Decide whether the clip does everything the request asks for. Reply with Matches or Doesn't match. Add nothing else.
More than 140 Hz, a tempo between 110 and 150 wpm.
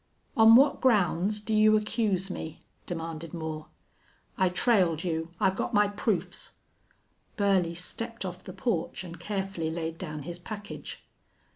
Matches